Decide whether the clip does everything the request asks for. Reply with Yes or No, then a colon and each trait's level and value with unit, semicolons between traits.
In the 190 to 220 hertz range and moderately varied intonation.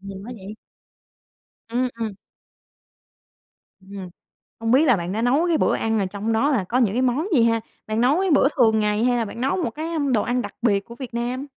No: high, 235 Hz; average, 3.3 semitones